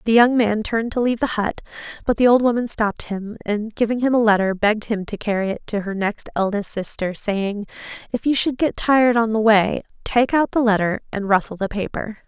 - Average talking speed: No, fast, 225 wpm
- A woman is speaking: Yes, female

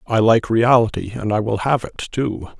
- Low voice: Yes, low, 115 Hz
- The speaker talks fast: Yes, fast, 210 wpm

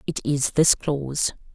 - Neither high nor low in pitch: Yes, medium, 145 Hz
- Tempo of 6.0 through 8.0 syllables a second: No, 4.1 syllables/s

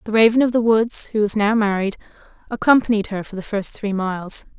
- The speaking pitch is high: Yes, high, 210 Hz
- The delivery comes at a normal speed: No, fast, 210 wpm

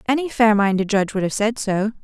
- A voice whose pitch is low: No, high, 215 Hz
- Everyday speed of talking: No, fast, 235 wpm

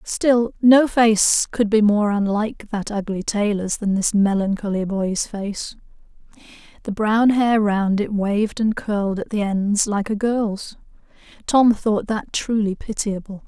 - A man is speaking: No, female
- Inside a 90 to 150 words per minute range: Yes, average, 145 wpm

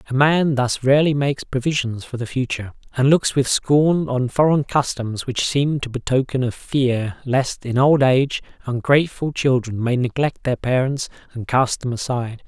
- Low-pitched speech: Yes, low, 130 Hz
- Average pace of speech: Yes, average, 175 wpm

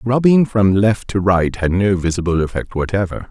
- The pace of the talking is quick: No, average, 180 wpm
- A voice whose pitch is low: Yes, low, 100 Hz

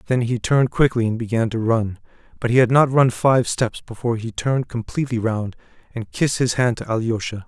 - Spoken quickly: Yes, fast, 210 wpm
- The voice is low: Yes, low, 120 Hz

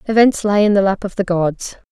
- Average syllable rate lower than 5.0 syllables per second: No, 5.4 syllables/s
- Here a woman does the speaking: Yes, female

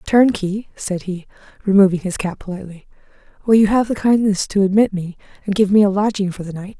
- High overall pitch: Yes, high, 200 Hz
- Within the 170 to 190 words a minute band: No, fast, 205 wpm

